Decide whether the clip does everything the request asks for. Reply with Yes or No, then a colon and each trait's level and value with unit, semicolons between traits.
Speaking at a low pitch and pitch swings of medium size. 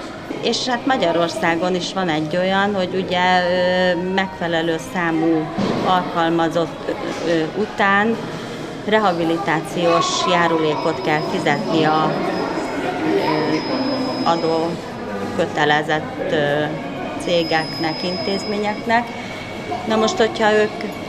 No: medium, 180 Hz; average, 4.2 semitones